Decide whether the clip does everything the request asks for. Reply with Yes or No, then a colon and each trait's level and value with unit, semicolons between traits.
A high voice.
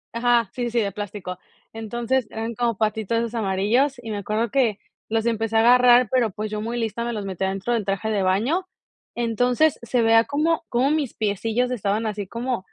Yes: high, 225 Hz